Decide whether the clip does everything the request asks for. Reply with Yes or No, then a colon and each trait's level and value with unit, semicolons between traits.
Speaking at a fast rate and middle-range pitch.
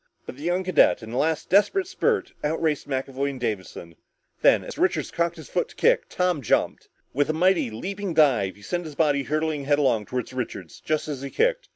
Yes: fast, 210 wpm; medium, 150 Hz